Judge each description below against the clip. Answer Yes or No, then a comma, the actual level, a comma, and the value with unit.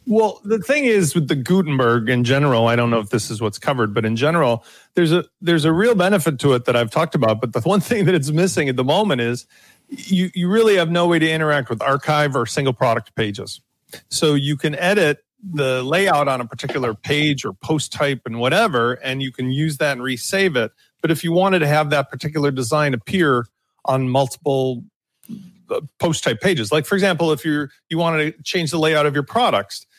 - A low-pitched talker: No, medium, 150 Hz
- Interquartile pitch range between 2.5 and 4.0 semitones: No, average, 5.0 semitones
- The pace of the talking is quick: Yes, fast, 220 wpm